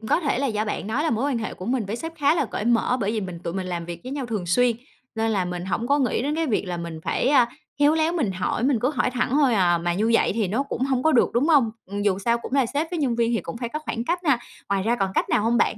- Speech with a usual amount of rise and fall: No, wide, 5.7 semitones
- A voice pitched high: Yes, high, 235 Hz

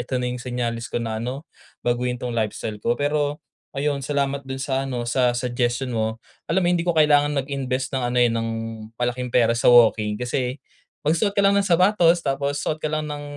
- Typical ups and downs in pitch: Yes, average, 3.2 semitones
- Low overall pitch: Yes, low, 130 Hz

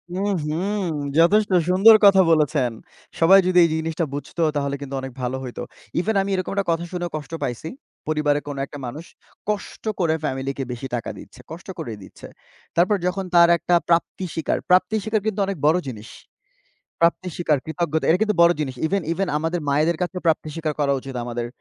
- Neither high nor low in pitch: Yes, medium, 165 Hz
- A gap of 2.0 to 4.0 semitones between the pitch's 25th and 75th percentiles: No, average, 4.4 semitones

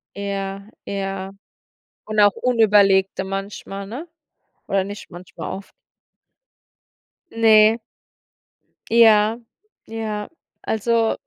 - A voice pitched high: Yes, high, 205 Hz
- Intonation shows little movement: Yes, narrow, 2.2 semitones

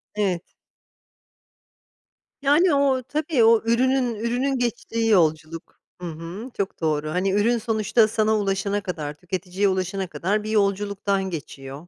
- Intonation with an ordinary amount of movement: Yes, average, 4.5 semitones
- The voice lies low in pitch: No, high, 205 Hz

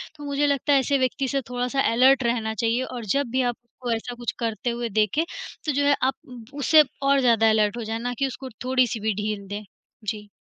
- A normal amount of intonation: Yes, average, 3.3 semitones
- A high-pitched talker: Yes, high, 245 Hz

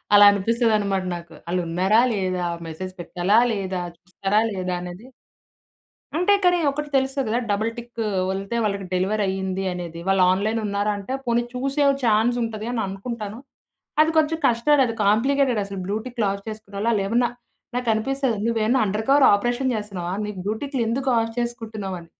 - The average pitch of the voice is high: Yes, high, 215 Hz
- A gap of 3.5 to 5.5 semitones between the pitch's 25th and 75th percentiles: Yes, average, 3.8 semitones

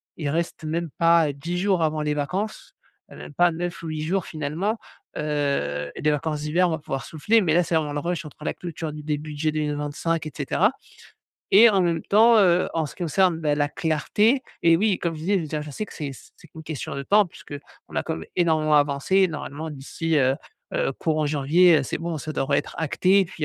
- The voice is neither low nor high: Yes, medium, 160 Hz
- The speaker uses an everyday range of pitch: Yes, average, 3.0 semitones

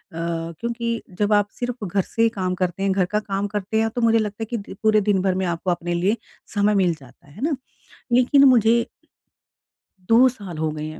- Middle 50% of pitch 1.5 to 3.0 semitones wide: No, average, 3.9 semitones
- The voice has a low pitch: No, high, 205 Hz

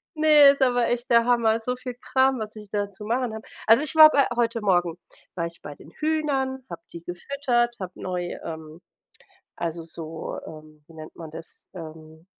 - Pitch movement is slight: No, wide, 7.2 semitones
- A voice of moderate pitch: No, high, 220 Hz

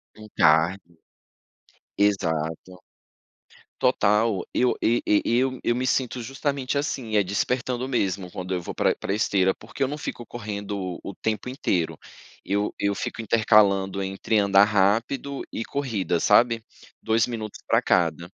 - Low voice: Yes, low, 105 Hz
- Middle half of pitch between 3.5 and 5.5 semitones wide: Yes, average, 3.9 semitones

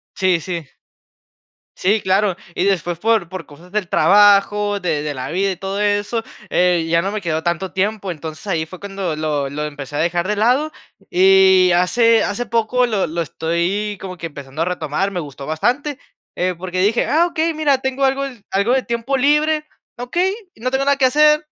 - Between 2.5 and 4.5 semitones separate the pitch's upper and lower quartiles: No, wide, 5.5 semitones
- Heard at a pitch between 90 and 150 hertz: No, high, 195 Hz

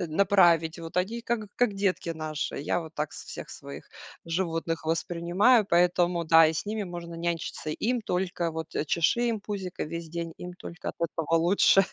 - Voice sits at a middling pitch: Yes, medium, 170 Hz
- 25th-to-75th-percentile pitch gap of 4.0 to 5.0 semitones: No, average, 2.8 semitones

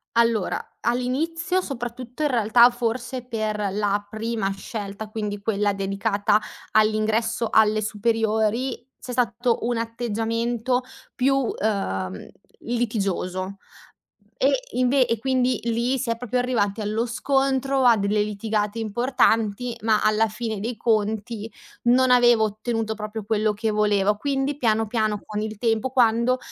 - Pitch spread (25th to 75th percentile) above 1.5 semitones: Yes, narrow, 2.5 semitones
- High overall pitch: Yes, high, 225 Hz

